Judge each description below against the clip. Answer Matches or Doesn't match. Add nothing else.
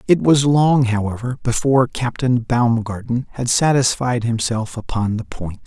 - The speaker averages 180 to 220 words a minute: Doesn't match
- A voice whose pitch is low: Matches